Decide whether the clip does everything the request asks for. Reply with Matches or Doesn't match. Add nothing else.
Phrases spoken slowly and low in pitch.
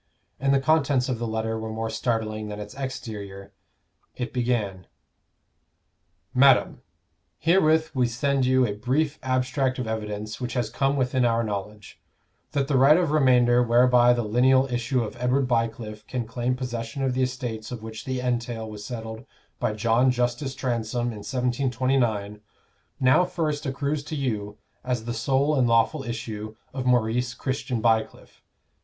Doesn't match